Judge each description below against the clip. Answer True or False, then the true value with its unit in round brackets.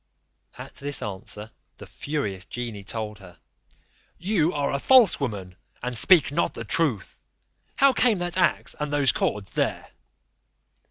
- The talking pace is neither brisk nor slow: True (145 wpm)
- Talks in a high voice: False (140 Hz)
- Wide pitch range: True (8.1 semitones)